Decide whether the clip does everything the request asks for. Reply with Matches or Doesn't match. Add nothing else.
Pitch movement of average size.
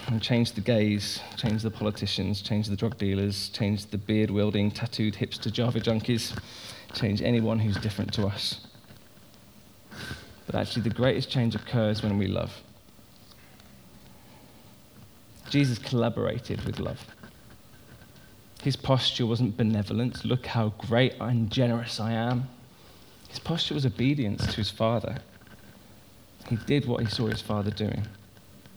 Doesn't match